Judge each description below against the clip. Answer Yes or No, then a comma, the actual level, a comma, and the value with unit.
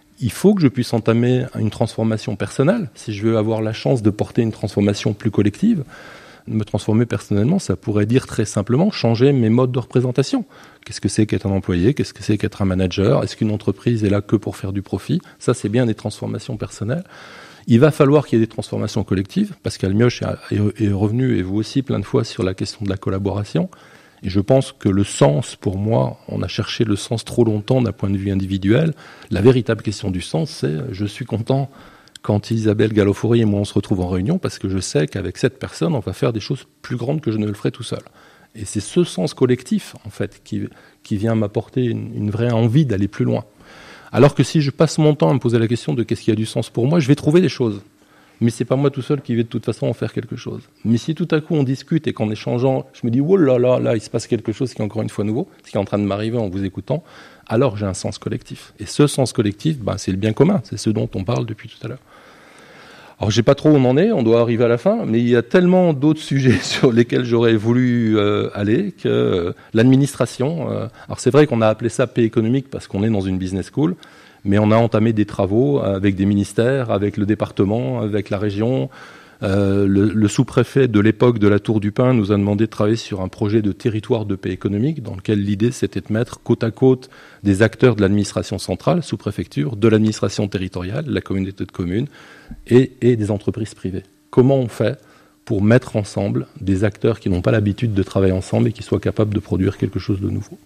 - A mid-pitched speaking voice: No, low, 115 Hz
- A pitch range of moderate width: Yes, average, 3.8 semitones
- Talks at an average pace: No, fast, 245 wpm